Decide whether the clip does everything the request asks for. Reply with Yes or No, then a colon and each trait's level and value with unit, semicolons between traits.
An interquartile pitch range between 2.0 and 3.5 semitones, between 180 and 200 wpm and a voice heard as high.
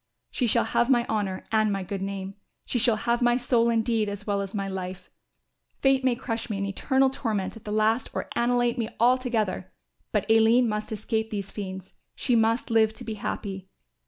Yes: average, 3.0 semitones; average, 195 wpm; high, 220 Hz